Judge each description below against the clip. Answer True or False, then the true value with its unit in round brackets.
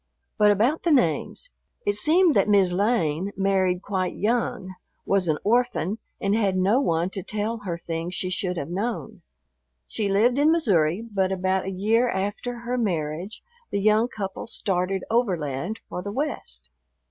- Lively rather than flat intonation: False (3.9 semitones)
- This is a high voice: True (200 Hz)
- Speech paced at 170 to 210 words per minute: False (160 wpm)